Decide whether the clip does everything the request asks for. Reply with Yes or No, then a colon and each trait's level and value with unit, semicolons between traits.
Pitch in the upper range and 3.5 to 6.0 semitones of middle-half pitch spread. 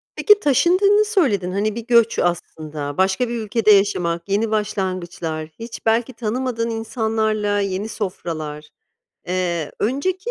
Yes: high, 210 Hz; average, 4.5 semitones